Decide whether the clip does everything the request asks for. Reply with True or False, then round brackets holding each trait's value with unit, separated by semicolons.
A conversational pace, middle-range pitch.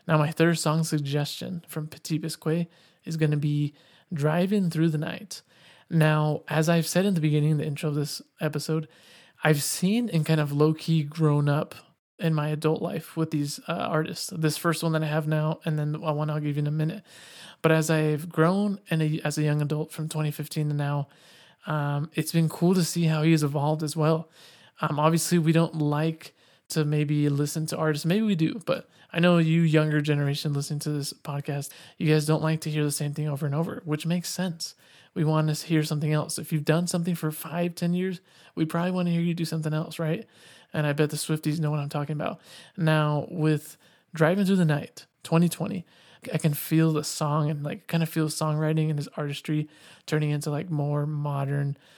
False (215 wpm; 155 Hz)